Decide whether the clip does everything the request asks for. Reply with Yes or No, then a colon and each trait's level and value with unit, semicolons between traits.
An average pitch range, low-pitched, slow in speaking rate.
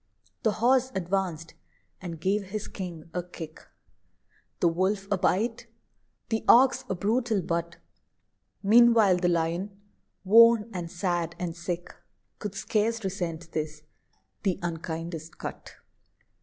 No: average, 3.8 semitones; medium, 185 Hz; slow, 120 wpm